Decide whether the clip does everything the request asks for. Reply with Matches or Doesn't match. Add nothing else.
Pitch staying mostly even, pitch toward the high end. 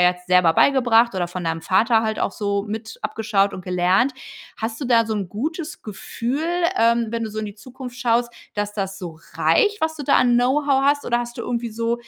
Doesn't match